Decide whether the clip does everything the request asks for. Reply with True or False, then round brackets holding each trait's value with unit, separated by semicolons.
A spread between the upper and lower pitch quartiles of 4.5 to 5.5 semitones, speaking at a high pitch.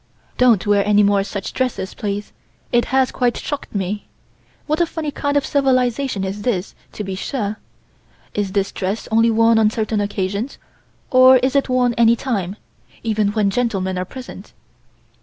False (4.1 semitones; 220 Hz)